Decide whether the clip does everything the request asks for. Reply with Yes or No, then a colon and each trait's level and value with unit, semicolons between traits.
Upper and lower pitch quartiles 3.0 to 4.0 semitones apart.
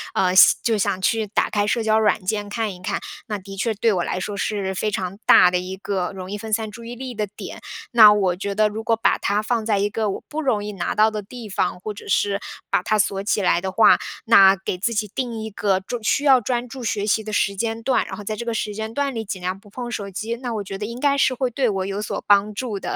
No: narrow, 2.4 semitones